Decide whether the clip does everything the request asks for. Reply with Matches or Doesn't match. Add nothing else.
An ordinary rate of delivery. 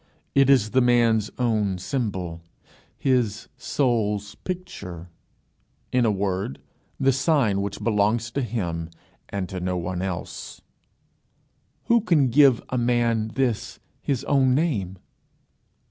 Doesn't match